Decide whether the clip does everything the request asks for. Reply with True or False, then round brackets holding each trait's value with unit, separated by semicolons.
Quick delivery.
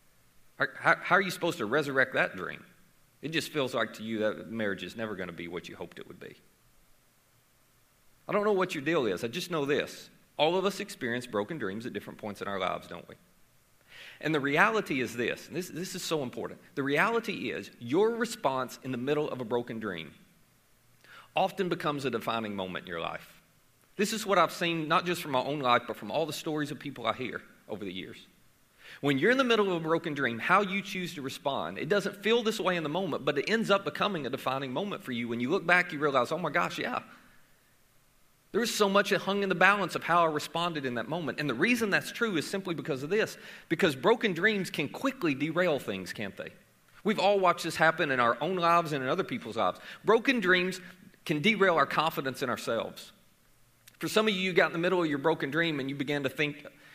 True (235 wpm)